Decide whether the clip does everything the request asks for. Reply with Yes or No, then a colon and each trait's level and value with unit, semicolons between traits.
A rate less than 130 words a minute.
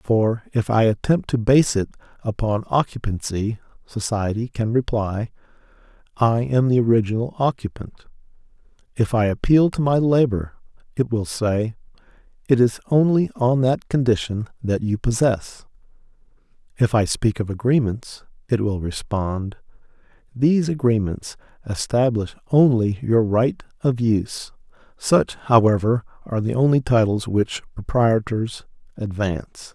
Yes: slow, 120 wpm